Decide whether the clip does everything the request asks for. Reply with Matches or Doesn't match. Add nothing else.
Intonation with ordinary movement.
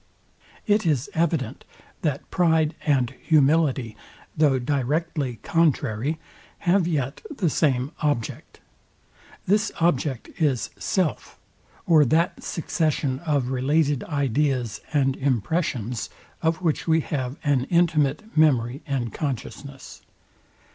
Matches